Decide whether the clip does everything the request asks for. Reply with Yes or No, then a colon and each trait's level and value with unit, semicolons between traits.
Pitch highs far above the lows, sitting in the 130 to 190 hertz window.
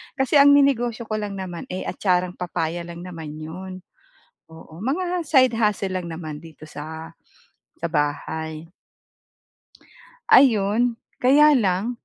Yes: wide, 6.9 semitones; medium, 185 Hz